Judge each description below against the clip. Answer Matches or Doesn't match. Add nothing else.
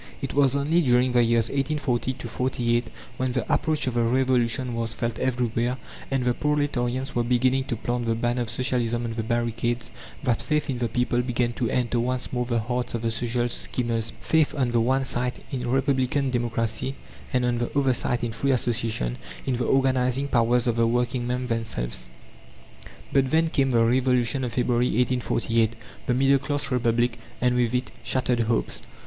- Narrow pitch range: Matches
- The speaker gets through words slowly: Doesn't match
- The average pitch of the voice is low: Matches